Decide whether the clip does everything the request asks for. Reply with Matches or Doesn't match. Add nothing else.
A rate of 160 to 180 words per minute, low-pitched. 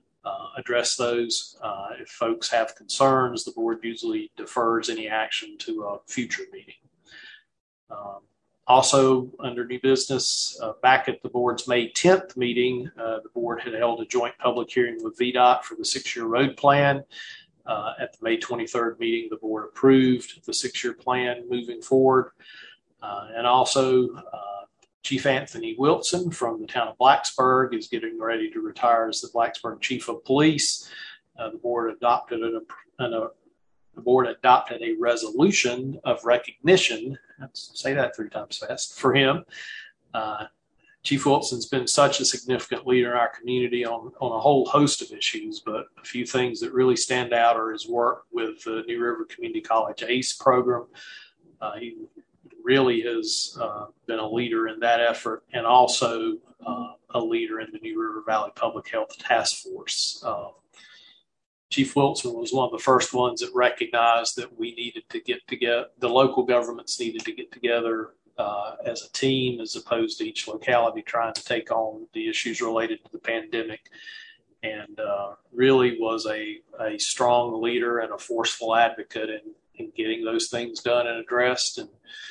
Matches